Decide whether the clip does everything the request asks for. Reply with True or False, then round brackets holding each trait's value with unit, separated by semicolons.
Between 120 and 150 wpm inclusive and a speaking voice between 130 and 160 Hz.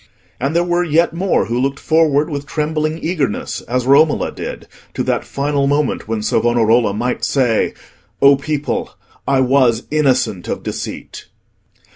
True (145 wpm; 140 Hz)